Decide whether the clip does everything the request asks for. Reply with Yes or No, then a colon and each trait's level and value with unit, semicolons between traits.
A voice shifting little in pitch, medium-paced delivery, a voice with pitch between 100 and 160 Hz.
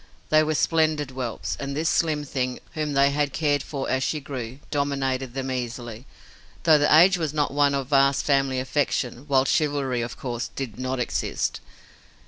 Yes: narrow, 2.3 semitones; average, 175 wpm; medium, 140 Hz